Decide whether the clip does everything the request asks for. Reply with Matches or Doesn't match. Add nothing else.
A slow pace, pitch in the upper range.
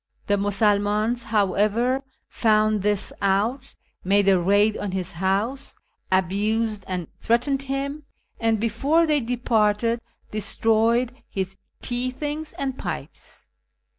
Matches